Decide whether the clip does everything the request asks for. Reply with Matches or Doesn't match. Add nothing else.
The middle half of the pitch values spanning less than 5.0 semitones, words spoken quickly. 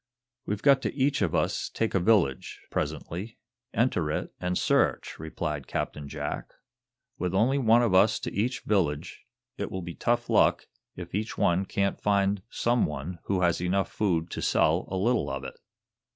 Doesn't match